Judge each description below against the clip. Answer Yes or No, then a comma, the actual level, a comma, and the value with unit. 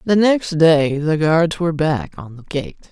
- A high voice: No, medium, 160 Hz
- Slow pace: No, fast, 205 wpm